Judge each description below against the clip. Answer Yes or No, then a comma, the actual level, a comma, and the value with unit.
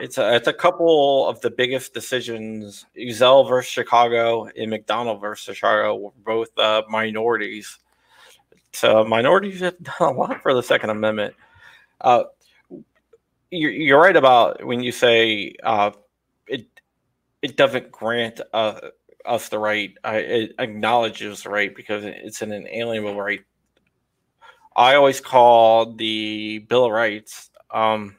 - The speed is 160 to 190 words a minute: No, average, 140 wpm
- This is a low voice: Yes, low, 115 Hz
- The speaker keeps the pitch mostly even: No, average, 3.0 semitones